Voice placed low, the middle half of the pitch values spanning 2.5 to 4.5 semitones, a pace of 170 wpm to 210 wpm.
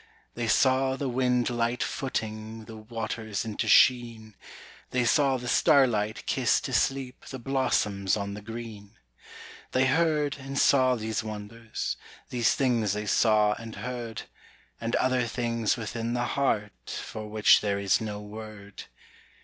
No: low, 115 Hz; average, 2.9 semitones; average, 140 wpm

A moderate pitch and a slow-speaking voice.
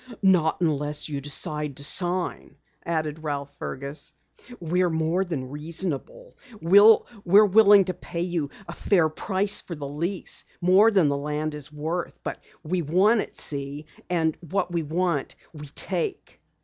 No: medium, 165 Hz; average, 150 wpm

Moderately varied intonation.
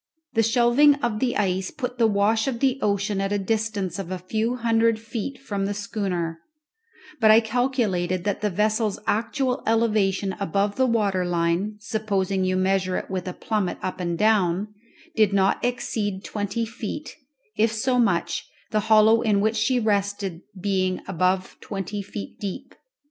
Yes: average, 3.0 semitones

